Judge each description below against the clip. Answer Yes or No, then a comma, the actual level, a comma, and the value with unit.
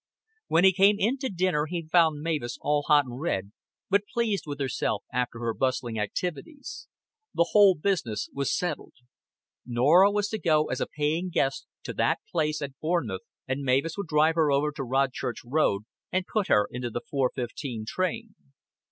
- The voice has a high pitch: No, medium, 150 Hz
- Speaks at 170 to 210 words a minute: Yes, average, 180 wpm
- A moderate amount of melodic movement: No, wide, 6.0 semitones